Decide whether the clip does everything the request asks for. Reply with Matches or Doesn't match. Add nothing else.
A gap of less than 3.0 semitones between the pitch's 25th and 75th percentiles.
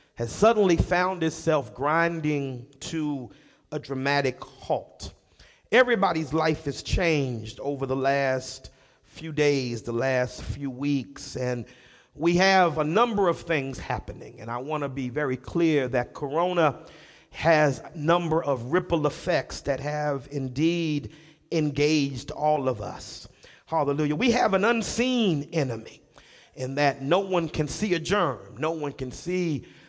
Doesn't match